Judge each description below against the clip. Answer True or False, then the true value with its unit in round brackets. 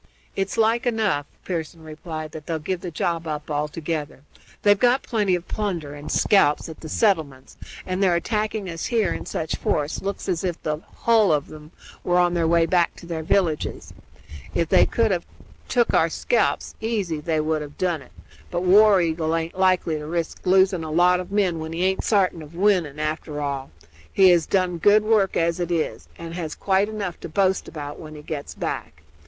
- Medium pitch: True (170 Hz)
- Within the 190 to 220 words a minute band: True (200 wpm)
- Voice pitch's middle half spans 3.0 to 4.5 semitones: True (3.6 semitones)